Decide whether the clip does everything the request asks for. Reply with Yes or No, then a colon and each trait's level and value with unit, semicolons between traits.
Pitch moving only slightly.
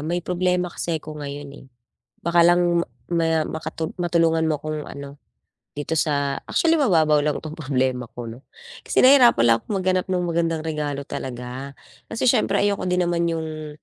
No: average, 3.2 semitones